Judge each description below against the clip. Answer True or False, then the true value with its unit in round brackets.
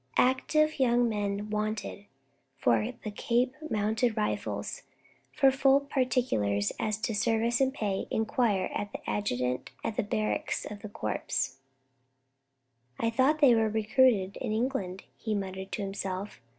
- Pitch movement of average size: True (3.8 semitones)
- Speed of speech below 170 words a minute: True (140 wpm)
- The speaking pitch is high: True (215 Hz)